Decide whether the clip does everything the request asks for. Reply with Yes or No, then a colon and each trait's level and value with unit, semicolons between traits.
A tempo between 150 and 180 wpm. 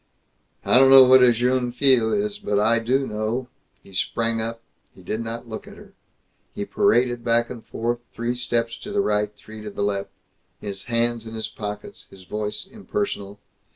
No: average, 190 wpm